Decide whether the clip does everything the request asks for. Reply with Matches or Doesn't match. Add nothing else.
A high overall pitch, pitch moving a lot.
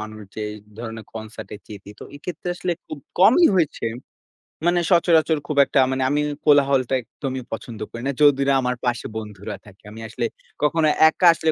Doesn't match